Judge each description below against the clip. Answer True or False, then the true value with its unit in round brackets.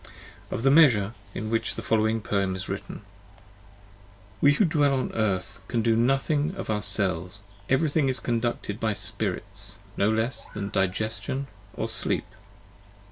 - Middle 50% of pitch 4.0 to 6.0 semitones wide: True (4.9 semitones)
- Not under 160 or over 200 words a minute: False (150 wpm)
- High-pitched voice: False (110 Hz)